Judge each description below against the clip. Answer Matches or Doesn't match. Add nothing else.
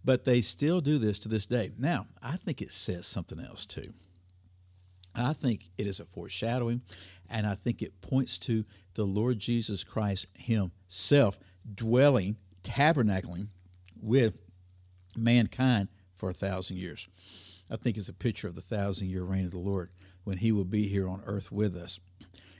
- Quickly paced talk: Doesn't match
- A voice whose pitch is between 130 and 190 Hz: Doesn't match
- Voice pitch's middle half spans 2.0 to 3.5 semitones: Doesn't match